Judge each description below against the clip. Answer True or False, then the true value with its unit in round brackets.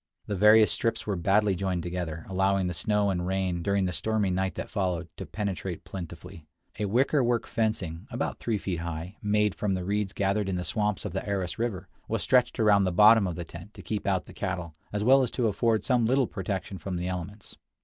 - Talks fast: True (215 wpm)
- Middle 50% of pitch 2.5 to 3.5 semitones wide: True (2.9 semitones)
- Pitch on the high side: False (100 Hz)